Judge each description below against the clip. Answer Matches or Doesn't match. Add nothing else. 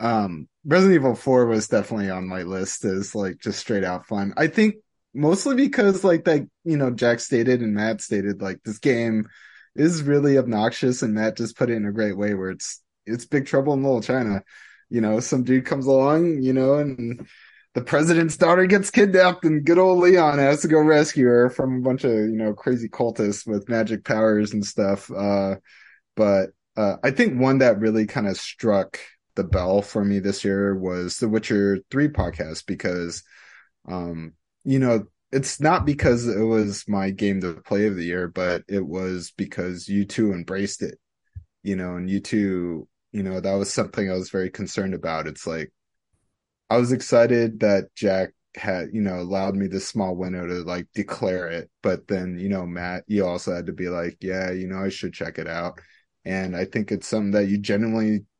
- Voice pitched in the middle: Doesn't match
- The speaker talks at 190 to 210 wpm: Matches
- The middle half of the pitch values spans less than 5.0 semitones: Doesn't match